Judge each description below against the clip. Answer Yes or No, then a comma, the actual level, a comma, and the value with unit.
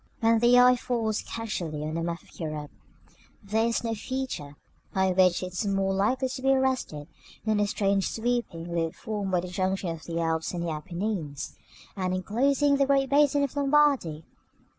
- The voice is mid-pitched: No, high, 200 Hz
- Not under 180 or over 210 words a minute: Yes, average, 185 wpm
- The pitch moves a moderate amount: No, wide, 6.5 semitones